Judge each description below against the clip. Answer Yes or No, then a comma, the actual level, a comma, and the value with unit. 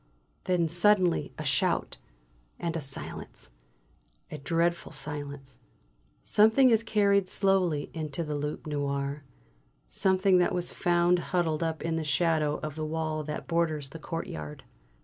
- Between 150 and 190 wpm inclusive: No, slow, 135 wpm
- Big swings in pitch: No, average, 3.2 semitones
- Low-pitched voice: No, medium, 160 Hz